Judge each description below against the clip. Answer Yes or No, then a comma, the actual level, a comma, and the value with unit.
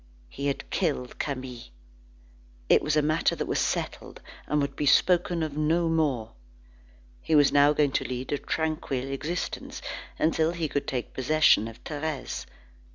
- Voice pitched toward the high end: No, medium, 150 Hz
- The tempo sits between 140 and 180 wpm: Yes, average, 160 wpm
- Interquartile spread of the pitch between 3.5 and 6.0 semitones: No, average, 2.7 semitones